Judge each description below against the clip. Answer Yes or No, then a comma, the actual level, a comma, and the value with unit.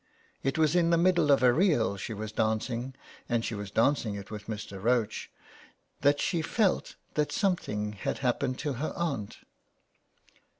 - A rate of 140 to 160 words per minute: No, average, 170 wpm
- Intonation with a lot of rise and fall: Yes, wide, 6.4 semitones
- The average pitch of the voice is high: No, low, 125 Hz